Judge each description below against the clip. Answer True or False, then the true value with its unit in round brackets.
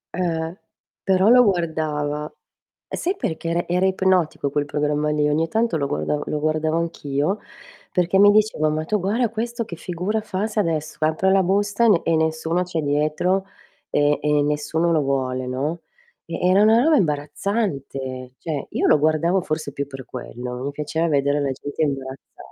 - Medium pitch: True (160 Hz)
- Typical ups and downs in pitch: True (4.3 semitones)